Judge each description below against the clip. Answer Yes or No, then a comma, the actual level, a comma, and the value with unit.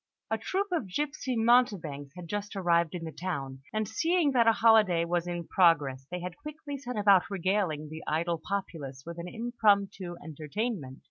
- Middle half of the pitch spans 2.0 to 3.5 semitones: No, average, 5.3 semitones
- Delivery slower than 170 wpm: No, average, 175 wpm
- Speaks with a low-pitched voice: No, medium, 185 Hz